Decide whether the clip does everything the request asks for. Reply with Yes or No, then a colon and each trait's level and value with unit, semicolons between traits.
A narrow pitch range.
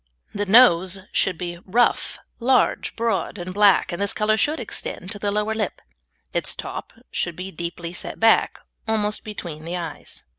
No: average, 3.8 semitones